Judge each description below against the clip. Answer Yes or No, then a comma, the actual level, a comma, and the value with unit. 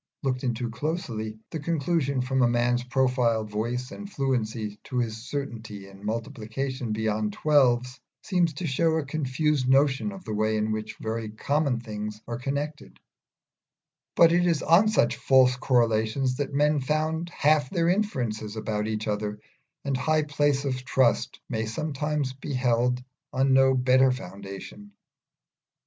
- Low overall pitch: Yes, low, 130 Hz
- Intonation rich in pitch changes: No, average, 4.7 semitones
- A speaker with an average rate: Yes, average, 150 wpm